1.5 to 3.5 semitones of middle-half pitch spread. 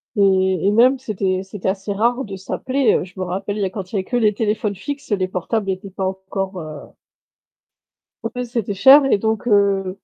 Yes: average, 2.8 semitones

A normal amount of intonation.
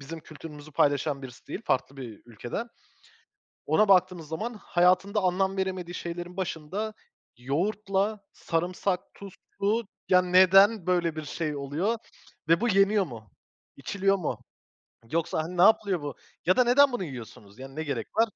Yes: average, 4.8 semitones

